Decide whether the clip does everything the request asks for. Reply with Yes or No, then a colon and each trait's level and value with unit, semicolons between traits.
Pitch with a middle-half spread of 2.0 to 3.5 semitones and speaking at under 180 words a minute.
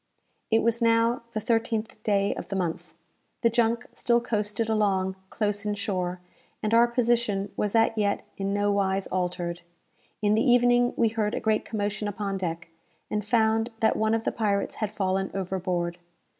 Yes: narrow, 2.6 semitones; average, 170 wpm